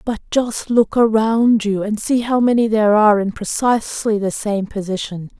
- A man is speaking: No, female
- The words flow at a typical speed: Yes, average, 180 wpm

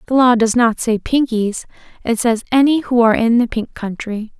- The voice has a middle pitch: No, high, 235 Hz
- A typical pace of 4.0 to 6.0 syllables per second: Yes, 5.1 syllables/s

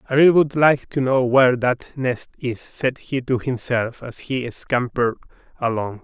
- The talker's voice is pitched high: No, low, 125 Hz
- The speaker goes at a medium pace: Yes, average, 180 wpm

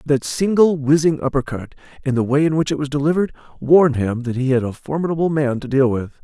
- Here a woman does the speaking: No, male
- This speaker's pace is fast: Yes, fast, 220 wpm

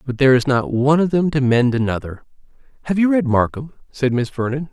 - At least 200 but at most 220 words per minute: Yes, fast, 205 wpm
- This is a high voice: No, low, 135 Hz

